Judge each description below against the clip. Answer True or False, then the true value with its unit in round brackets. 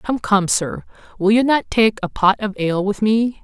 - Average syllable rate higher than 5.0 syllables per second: False (4.7 syllables/s)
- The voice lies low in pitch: False (210 Hz)